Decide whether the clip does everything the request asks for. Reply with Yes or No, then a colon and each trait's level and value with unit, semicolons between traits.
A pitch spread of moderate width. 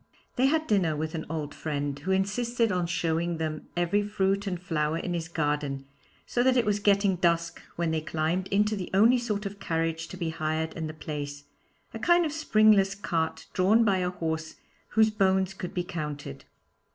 Yes: average, 4.2 semitones